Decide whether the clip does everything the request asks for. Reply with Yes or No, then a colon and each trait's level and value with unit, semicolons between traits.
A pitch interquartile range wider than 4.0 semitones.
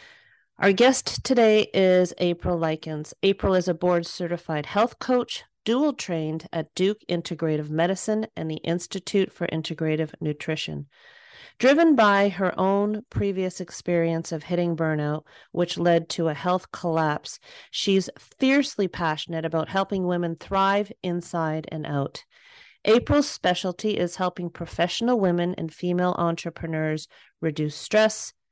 No: average, 3.6 semitones